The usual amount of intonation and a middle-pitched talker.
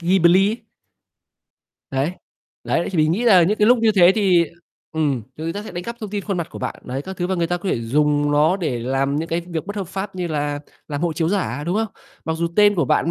Yes: average, 4.4 semitones; medium, 175 Hz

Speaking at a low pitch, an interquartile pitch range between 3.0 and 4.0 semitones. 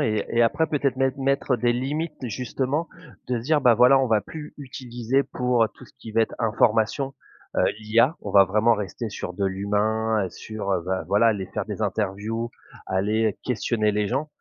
Yes: low, 115 Hz; average, 3.6 semitones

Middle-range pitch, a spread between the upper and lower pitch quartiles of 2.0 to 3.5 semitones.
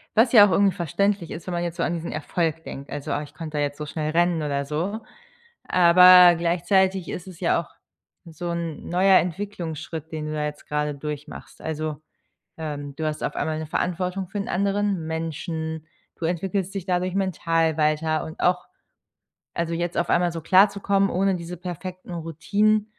Yes: medium, 170 Hz; average, 2.8 semitones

